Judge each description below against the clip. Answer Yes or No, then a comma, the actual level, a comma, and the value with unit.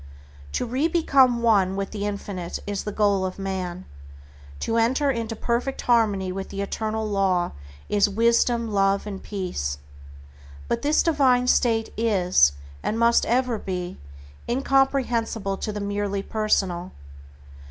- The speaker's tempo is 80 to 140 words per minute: Yes, slow, 135 wpm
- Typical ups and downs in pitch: Yes, average, 3.3 semitones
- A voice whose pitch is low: No, high, 210 Hz